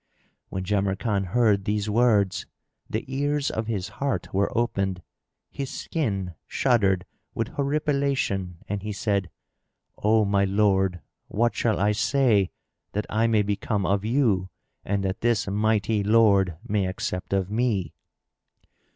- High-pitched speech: No, low, 105 Hz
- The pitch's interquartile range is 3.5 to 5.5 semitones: No, average, 3.0 semitones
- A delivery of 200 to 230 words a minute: No, slow, 135 wpm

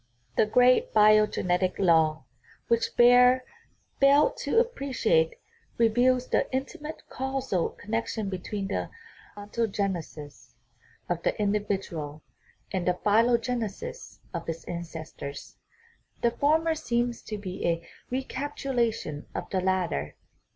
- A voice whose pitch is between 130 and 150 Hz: No, high, 215 Hz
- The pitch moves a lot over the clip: Yes, wide, 6.0 semitones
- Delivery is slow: Yes, slow, 110 wpm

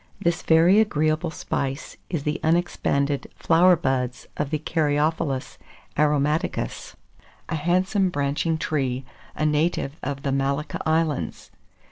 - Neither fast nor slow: No, slow, 115 wpm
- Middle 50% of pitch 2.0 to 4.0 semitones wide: Yes, average, 2.9 semitones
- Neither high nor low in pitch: Yes, medium, 155 Hz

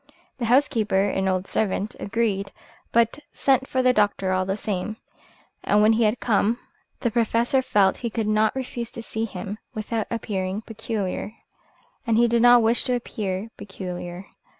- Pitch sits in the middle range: No, high, 220 Hz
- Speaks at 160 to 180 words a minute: Yes, average, 165 wpm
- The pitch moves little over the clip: No, average, 3.0 semitones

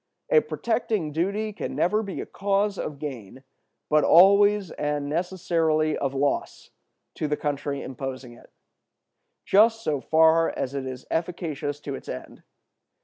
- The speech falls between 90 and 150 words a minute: Yes, average, 145 wpm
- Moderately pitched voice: Yes, medium, 160 Hz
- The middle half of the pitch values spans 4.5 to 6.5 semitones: Yes, wide, 5.6 semitones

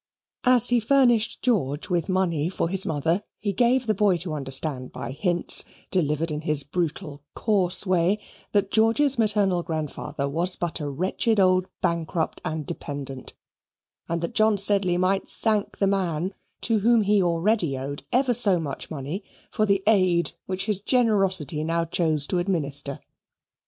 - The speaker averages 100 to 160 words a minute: Yes, average, 155 wpm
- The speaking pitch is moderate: Yes, medium, 180 Hz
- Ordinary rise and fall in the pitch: Yes, average, 4.9 semitones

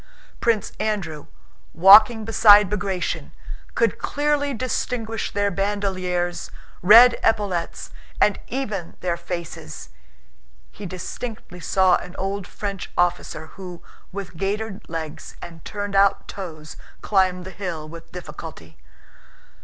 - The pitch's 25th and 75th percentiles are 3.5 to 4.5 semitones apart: No, average, 3.0 semitones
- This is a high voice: Yes, high, 195 Hz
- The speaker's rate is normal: No, slow, 110 wpm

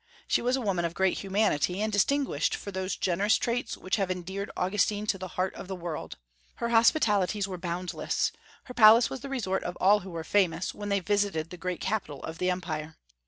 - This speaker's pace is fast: Yes, fast, 210 wpm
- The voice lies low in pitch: No, high, 190 Hz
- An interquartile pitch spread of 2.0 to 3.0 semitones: Yes, average, 2.7 semitones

